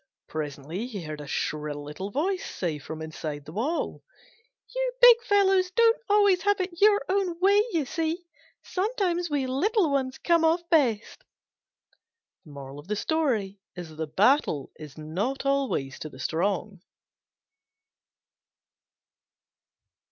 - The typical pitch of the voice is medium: No, very high, 270 Hz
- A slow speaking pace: Yes, slow, 115 wpm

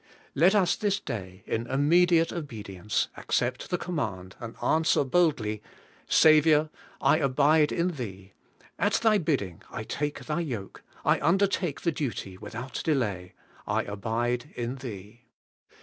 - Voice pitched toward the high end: No, low, 135 Hz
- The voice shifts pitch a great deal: Yes, wide, 7.1 semitones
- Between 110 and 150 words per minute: Yes, slow, 135 wpm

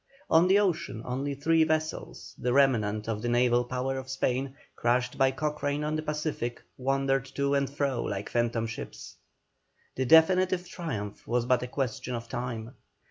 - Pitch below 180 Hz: Yes, low, 135 Hz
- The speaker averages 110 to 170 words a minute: Yes, average, 165 wpm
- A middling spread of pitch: Yes, average, 3.8 semitones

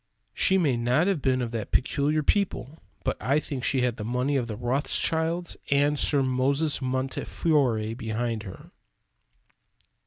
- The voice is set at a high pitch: No, low, 130 Hz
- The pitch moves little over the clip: No, average, 3.6 semitones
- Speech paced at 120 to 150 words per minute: Yes, average, 145 wpm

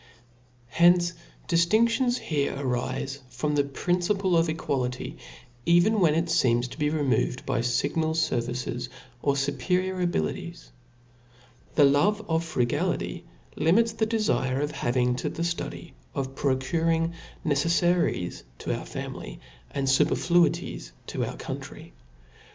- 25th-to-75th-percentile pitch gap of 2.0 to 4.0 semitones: No, average, 4.9 semitones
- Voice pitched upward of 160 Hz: No, medium, 155 Hz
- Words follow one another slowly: Yes, slow, 120 wpm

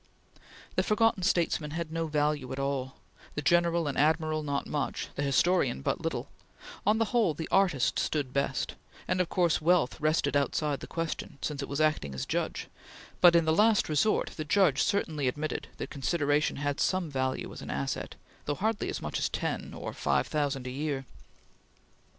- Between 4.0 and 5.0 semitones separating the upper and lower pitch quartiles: No, average, 3.5 semitones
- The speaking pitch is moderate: Yes, medium, 155 Hz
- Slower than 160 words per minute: No, average, 180 wpm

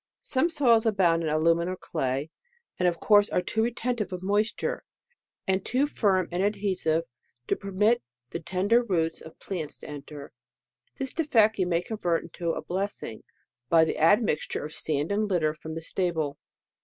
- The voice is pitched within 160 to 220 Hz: Yes, medium, 185 Hz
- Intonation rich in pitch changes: No, average, 4.5 semitones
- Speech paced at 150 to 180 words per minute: Yes, average, 170 wpm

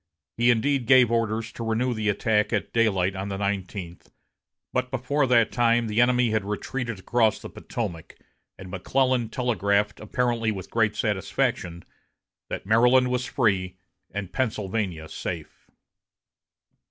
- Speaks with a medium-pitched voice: No, low, 110 Hz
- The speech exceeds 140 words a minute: No, slow, 135 wpm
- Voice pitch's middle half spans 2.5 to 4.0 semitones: Yes, average, 3.3 semitones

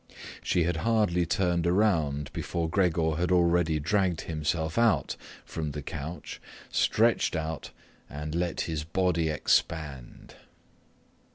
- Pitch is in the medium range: No, very low, 85 Hz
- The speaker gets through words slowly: Yes, slow, 115 wpm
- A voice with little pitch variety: Yes, narrow, 2.3 semitones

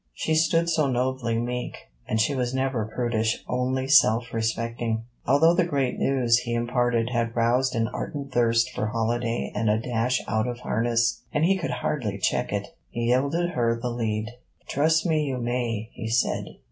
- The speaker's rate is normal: Yes, average, 175 wpm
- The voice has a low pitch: Yes, low, 120 Hz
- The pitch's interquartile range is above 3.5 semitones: No, narrow, 2.4 semitones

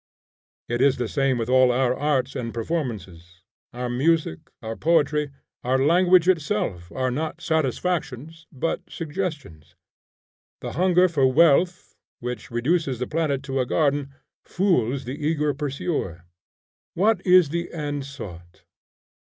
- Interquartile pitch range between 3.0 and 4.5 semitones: No, average, 4.9 semitones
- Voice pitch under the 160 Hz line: Yes, medium, 140 Hz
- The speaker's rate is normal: No, slow, 130 wpm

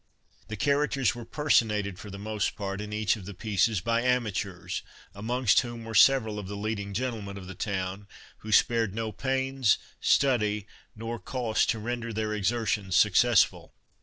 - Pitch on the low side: Yes, low, 110 Hz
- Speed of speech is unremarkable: Yes, average, 165 wpm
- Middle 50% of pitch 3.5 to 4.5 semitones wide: No, average, 2.8 semitones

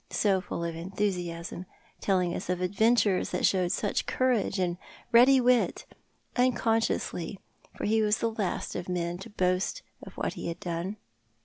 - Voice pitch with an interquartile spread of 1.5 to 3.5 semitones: No, average, 3.9 semitones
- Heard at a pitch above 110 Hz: Yes, high, 190 Hz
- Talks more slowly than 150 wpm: No, average, 155 wpm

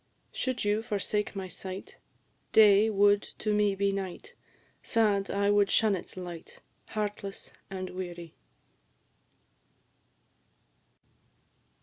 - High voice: Yes, high, 200 Hz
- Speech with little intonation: Yes, narrow, 1.7 semitones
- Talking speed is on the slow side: Yes, slow, 100 wpm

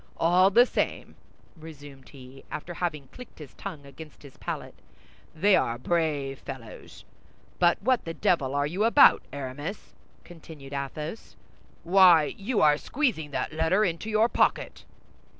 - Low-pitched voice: No, medium, 160 Hz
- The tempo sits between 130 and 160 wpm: Yes, average, 140 wpm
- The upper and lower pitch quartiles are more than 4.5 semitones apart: Yes, average, 4.9 semitones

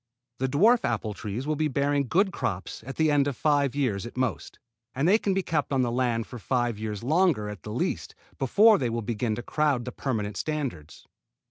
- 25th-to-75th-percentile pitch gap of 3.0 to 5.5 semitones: Yes, average, 4.8 semitones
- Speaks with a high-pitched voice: No, low, 130 Hz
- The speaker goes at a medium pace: No, fast, 215 wpm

